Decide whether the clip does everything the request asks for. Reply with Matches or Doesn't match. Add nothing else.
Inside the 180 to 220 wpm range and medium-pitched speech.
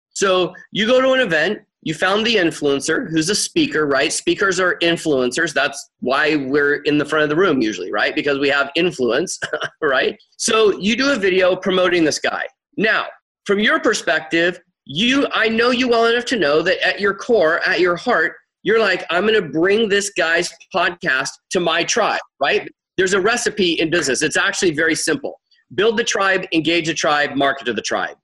Matches